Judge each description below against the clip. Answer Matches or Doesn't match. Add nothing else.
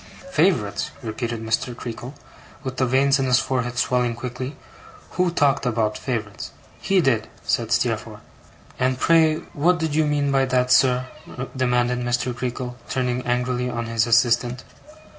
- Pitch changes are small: Matches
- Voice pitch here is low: Matches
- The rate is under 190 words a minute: Matches